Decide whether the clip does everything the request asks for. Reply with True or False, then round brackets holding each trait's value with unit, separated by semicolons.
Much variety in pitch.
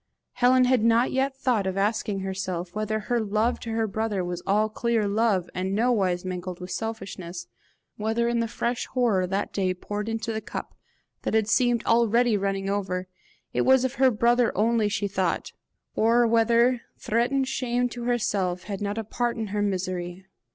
False (3.4 semitones)